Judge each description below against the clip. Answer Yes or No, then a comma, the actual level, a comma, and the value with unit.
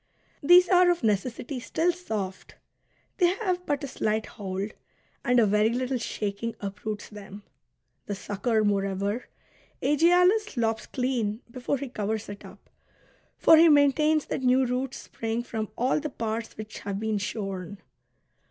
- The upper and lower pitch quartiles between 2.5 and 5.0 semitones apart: No, wide, 5.4 semitones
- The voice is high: Yes, high, 230 Hz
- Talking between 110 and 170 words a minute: Yes, average, 145 wpm